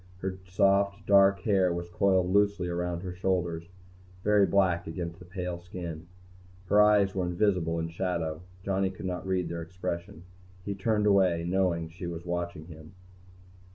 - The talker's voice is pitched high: No, very low, 90 Hz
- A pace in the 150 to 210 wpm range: Yes, average, 160 wpm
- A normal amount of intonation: No, narrow, 2.2 semitones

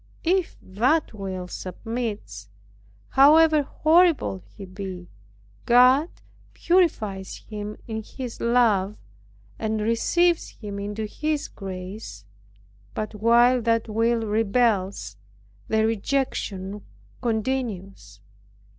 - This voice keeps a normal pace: No, slow, 95 wpm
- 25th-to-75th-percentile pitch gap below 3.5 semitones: No, average, 4.1 semitones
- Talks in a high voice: Yes, high, 220 Hz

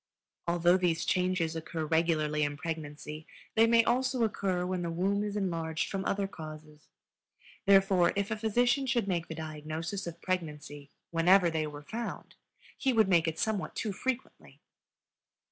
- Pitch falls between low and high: Yes, medium, 175 Hz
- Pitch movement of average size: Yes, average, 4.1 semitones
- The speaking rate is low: No, average, 155 wpm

